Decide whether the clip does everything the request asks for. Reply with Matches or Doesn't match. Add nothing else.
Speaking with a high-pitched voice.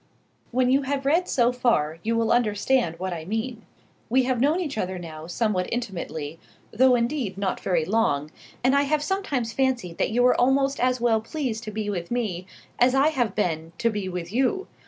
Matches